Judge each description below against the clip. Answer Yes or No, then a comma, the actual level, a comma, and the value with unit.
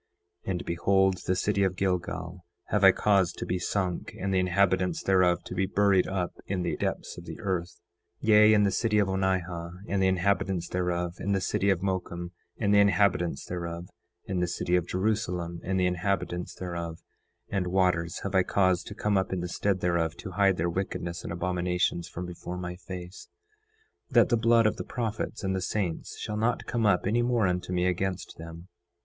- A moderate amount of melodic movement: No, narrow, 2.0 semitones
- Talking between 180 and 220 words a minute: Yes, average, 200 wpm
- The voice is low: Yes, very low, 95 Hz